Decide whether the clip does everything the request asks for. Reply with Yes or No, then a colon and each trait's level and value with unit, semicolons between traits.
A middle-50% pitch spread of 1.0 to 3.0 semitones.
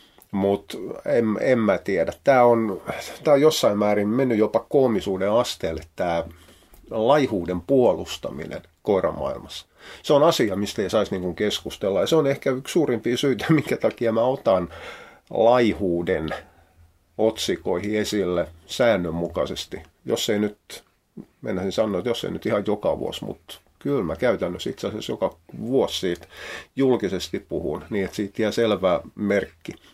No: average, 4.4 semitones